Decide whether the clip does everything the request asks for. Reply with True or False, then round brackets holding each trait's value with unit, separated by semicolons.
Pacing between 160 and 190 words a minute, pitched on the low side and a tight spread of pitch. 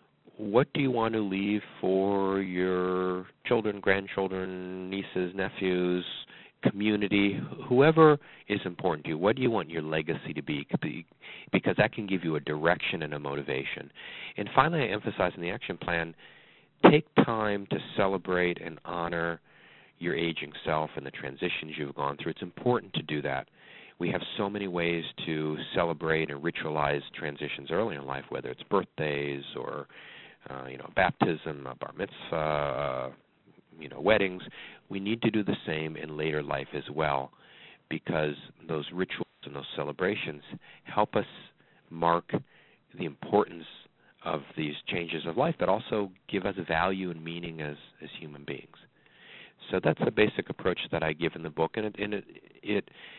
False (165 wpm; 85 Hz; 4.1 semitones)